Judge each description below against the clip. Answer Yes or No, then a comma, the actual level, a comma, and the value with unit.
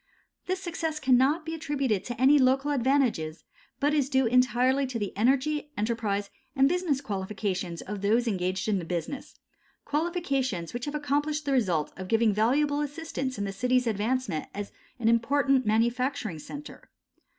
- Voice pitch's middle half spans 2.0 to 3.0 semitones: No, wide, 5.5 semitones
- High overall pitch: Yes, very high, 255 Hz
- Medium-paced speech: Yes, average, 155 wpm